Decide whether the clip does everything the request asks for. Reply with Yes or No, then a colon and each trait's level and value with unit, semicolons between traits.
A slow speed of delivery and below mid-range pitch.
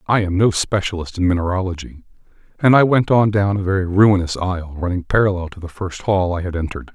No: fast, 205 wpm; very low, 95 Hz